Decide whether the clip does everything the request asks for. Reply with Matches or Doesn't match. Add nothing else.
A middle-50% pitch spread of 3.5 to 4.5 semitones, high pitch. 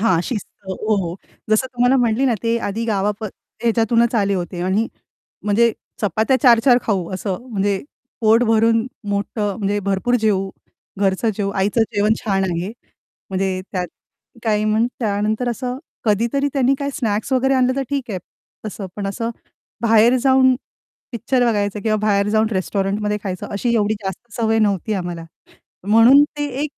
Doesn't match